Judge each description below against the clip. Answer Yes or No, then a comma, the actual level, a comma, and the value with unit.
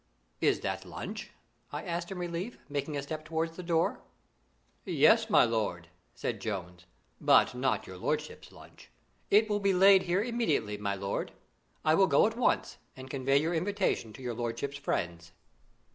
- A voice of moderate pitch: Yes, medium, 155 Hz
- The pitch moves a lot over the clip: Yes, wide, 8.4 semitones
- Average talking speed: Yes, average, 165 wpm